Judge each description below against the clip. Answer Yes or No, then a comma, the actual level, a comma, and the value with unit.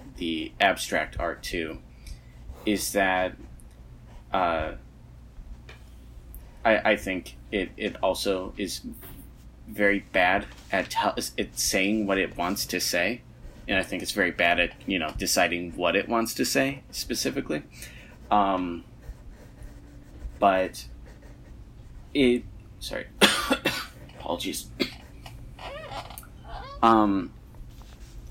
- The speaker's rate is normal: No, slow, 100 wpm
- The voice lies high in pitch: No, very low, 80 Hz